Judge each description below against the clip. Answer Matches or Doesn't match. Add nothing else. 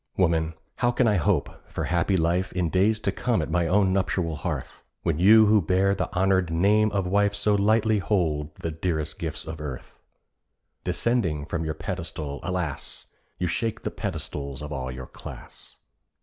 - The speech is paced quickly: Doesn't match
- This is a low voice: Matches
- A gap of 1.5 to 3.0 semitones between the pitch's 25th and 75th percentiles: Doesn't match